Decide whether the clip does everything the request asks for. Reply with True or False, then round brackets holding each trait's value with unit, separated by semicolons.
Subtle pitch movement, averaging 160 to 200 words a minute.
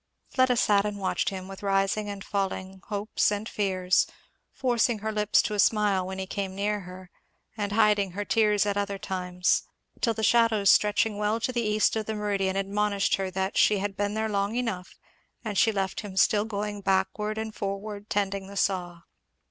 True (1.6 semitones; 190 wpm)